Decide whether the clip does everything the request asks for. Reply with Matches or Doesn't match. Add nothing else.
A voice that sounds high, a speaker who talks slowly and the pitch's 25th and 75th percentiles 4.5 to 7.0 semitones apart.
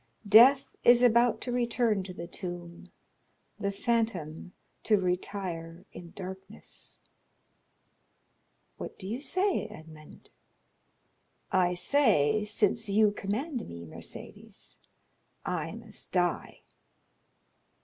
Matches